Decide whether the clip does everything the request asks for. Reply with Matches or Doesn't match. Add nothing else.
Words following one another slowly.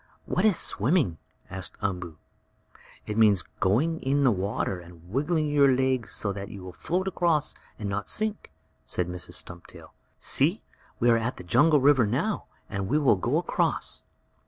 Doesn't match